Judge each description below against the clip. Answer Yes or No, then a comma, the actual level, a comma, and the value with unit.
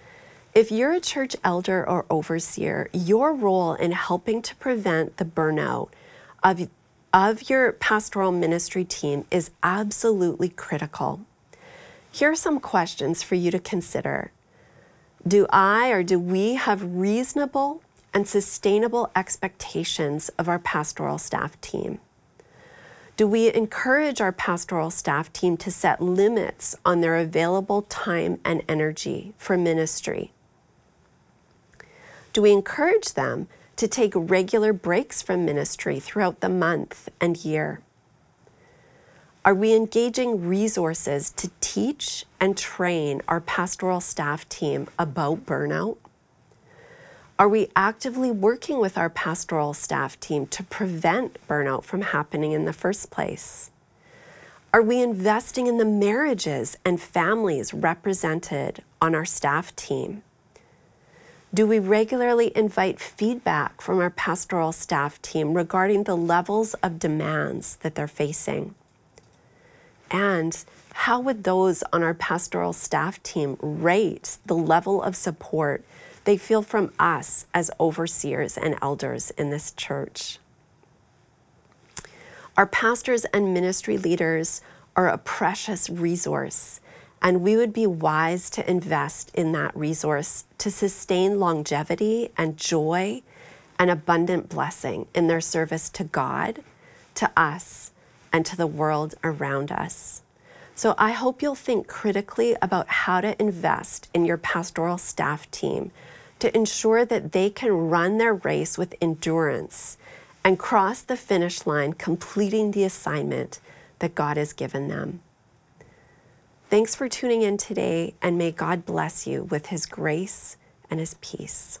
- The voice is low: No, medium, 180 Hz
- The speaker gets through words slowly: Yes, slow, 130 wpm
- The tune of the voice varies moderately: Yes, average, 4.6 semitones